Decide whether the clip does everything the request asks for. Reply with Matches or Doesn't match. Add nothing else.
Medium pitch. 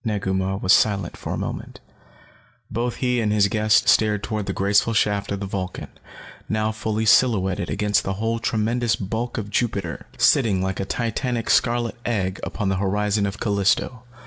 Doesn't match